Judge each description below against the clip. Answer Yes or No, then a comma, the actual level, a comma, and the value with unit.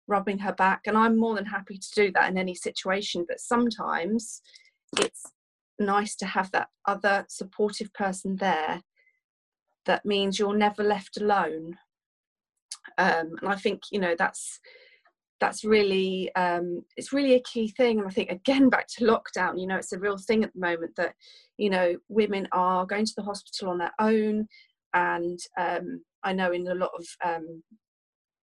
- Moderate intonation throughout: Yes, average, 3.3 semitones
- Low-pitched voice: No, high, 200 Hz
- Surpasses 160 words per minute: Yes, average, 175 wpm